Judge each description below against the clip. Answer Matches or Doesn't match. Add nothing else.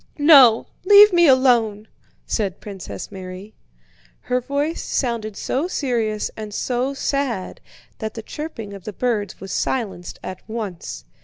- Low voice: Doesn't match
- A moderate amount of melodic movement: Matches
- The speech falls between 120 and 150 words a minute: Matches